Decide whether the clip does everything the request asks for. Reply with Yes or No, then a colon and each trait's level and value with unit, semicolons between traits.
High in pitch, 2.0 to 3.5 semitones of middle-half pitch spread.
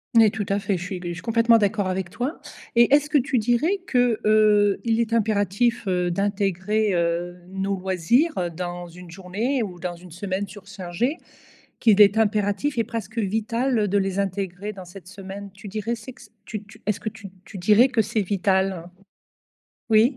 Yes: high, 205 Hz; average, 3.2 semitones